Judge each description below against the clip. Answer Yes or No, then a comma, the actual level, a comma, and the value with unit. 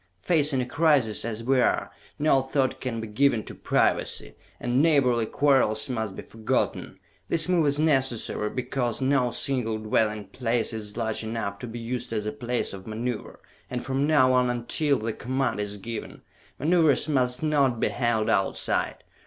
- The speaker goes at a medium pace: Yes, average, 170 wpm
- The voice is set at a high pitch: No, low, 125 Hz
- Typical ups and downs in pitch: Yes, average, 3.7 semitones